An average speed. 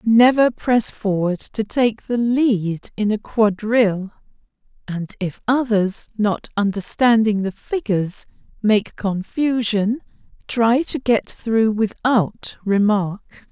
No: slow, 110 wpm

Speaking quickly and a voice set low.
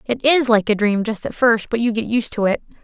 No: fast, 295 wpm; high, 225 Hz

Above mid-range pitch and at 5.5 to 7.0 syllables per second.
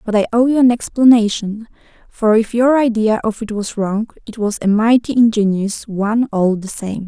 No: high, 220 Hz; 5.0 syllables/s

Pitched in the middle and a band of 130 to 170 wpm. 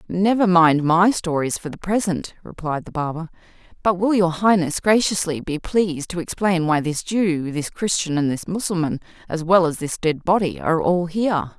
No: medium, 175 Hz; average, 185 wpm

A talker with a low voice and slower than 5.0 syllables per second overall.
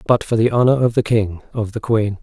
No: low, 110 Hz; 5.6 syllables/s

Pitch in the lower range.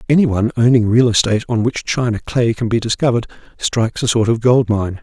Yes: low, 115 Hz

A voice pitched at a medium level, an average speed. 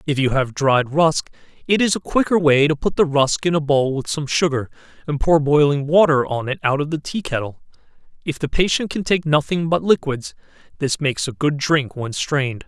No: medium, 145 Hz; fast, 220 wpm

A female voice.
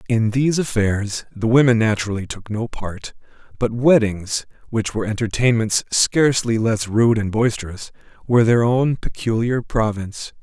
No: male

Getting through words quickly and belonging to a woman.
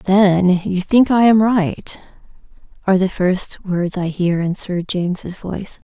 No: average, 165 wpm; female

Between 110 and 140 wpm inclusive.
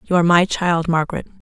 No: fast, 205 wpm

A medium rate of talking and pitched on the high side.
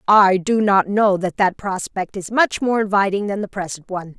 No: fast, 215 wpm; high, 195 Hz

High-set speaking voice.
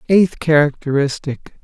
No: medium, 150 Hz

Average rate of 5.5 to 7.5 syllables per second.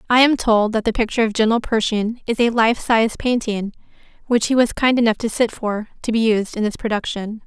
Yes: 5.8 syllables/s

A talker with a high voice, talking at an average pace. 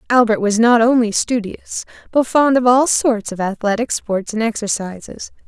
Yes: high, 230 Hz; average, 165 wpm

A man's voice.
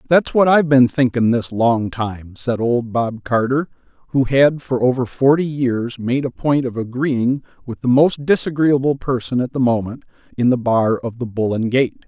Yes: male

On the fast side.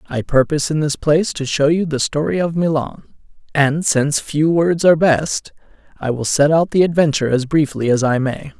No: average, 190 wpm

